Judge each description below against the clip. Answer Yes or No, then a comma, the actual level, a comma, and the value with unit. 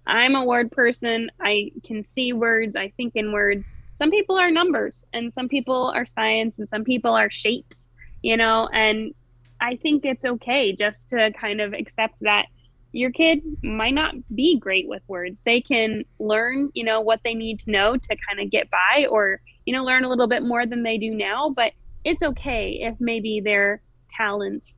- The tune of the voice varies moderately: Yes, average, 3.1 semitones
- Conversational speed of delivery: Yes, average, 195 wpm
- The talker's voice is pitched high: Yes, high, 225 Hz